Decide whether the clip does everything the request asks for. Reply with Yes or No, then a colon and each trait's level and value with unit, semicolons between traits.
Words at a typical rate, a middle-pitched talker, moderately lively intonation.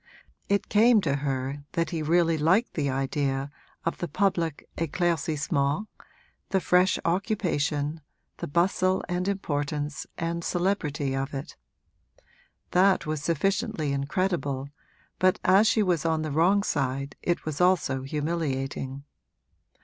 No: slow, 125 wpm; medium, 160 Hz; average, 4.5 semitones